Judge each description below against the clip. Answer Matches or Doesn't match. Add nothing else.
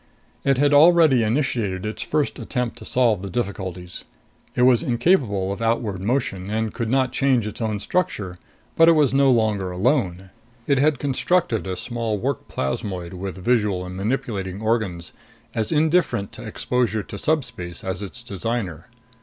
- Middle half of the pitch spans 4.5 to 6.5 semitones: Matches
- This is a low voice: Matches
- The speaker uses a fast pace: Doesn't match